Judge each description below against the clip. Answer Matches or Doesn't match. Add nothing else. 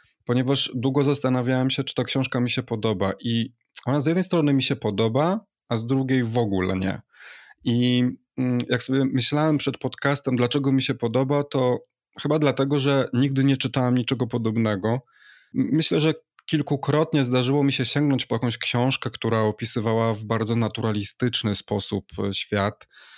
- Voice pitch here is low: Matches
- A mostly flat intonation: Doesn't match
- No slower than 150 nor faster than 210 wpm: Matches